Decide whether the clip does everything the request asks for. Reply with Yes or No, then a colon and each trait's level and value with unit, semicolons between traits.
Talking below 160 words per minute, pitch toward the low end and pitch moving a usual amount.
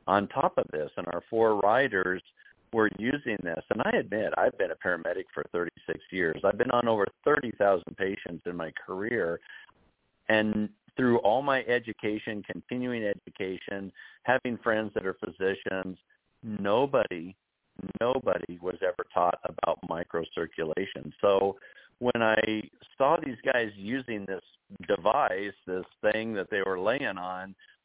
Yes: average, 140 wpm; low, 100 Hz; average, 3.5 semitones